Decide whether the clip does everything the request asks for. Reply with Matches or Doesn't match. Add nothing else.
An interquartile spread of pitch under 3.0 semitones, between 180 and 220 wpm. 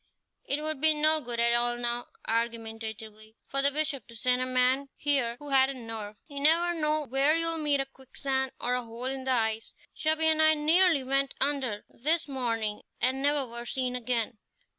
Doesn't match